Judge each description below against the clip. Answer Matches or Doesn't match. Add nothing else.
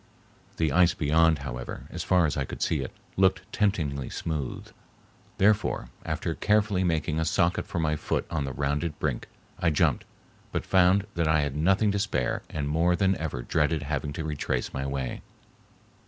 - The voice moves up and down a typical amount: Matches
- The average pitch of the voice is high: Doesn't match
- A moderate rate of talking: Matches